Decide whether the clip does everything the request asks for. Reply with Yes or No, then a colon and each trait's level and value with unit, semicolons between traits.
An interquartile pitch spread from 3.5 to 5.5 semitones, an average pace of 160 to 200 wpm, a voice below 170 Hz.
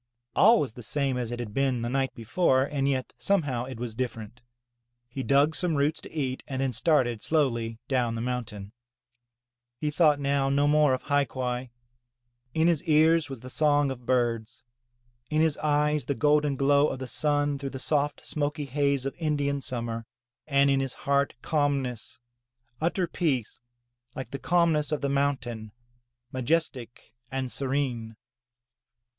No: average, 3.0 semitones; average, 165 wpm; medium, 140 Hz